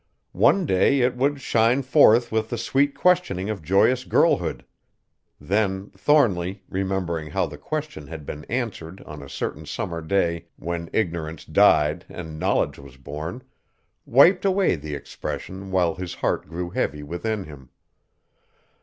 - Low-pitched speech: Yes, very low, 95 Hz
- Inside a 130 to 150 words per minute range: Yes, average, 145 wpm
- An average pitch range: No, wide, 6.9 semitones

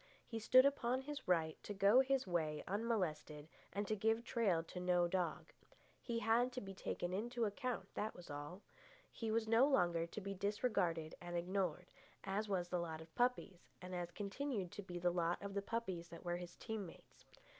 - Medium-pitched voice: No, high, 195 Hz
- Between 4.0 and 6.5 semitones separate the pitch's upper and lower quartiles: Yes, average, 4.5 semitones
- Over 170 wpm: Yes, average, 195 wpm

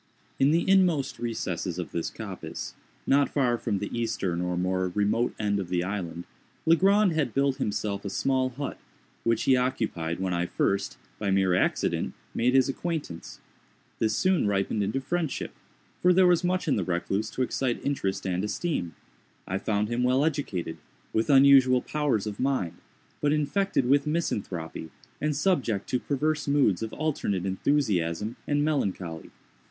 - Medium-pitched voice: No, low, 120 Hz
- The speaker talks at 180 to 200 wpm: No, average, 160 wpm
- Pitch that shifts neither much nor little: No, wide, 7.0 semitones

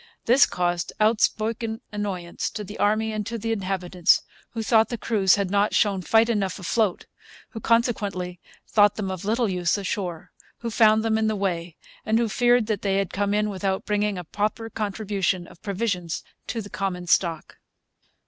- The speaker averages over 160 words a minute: Yes, average, 175 wpm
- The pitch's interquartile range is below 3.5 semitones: Yes, average, 2.9 semitones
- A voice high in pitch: Yes, high, 205 Hz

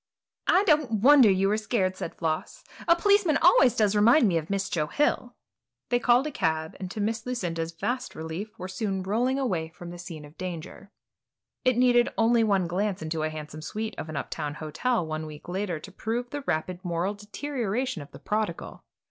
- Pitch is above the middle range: Yes, high, 200 Hz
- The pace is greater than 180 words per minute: Yes, average, 200 wpm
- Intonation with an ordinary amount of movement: No, wide, 6.5 semitones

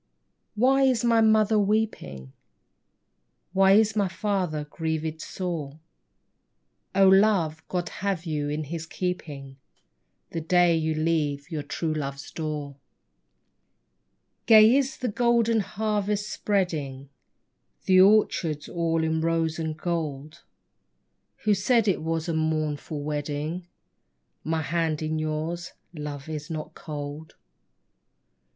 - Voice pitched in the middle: Yes, medium, 165 Hz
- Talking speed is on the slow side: Yes, slow, 125 wpm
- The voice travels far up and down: No, average, 4.4 semitones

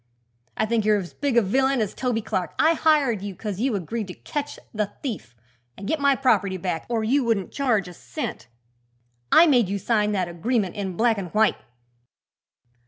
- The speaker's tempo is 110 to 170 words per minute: No, average, 190 wpm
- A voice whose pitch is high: Yes, high, 215 Hz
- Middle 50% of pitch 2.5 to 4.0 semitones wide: No, average, 4.8 semitones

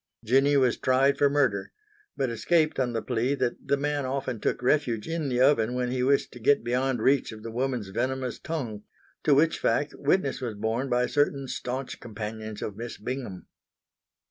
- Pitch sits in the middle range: No, low, 130 Hz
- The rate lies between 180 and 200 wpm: Yes, average, 185 wpm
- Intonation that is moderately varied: Yes, average, 3.1 semitones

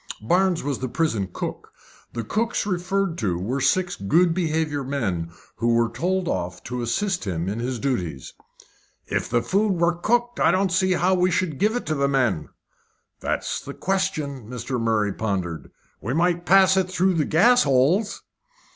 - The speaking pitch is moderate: Yes, medium, 155 Hz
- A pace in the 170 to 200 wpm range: Yes, average, 175 wpm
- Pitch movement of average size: No, wide, 8.0 semitones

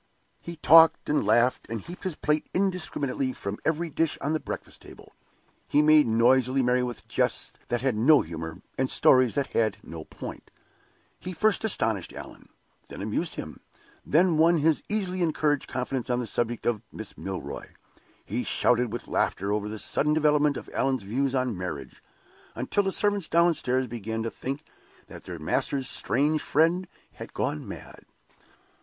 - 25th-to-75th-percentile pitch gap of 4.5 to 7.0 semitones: Yes, wide, 5.4 semitones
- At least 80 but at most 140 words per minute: No, average, 165 wpm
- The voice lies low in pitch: Yes, low, 130 Hz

